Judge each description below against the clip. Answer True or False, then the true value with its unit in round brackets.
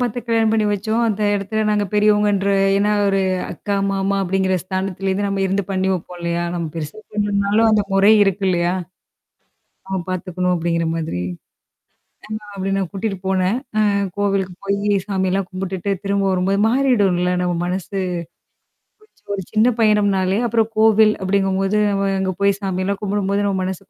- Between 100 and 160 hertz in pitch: False (195 Hz)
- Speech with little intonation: True (1.7 semitones)